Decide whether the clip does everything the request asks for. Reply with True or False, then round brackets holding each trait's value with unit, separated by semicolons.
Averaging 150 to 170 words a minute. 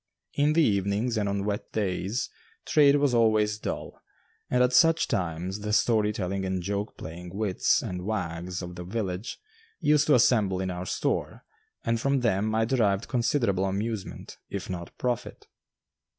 True (160 wpm)